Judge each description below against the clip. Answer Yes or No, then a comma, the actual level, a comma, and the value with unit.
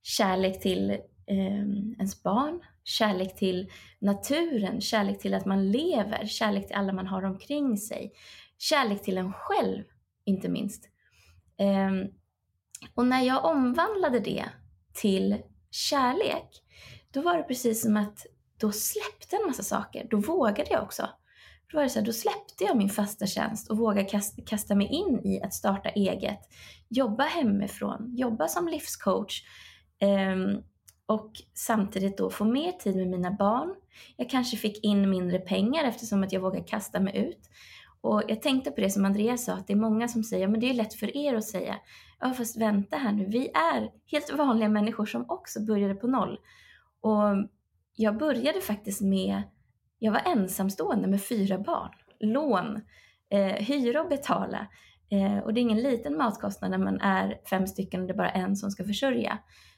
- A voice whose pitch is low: No, high, 210 Hz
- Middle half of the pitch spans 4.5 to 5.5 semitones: No, average, 4.0 semitones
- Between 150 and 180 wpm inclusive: Yes, average, 170 wpm